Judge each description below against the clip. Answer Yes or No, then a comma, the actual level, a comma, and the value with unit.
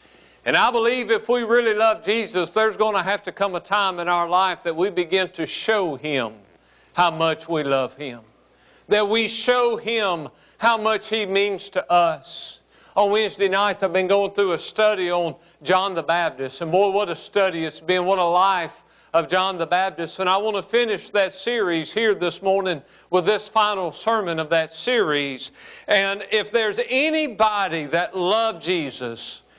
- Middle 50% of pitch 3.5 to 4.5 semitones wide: Yes, average, 4.1 semitones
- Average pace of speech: Yes, average, 185 wpm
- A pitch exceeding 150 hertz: Yes, high, 190 Hz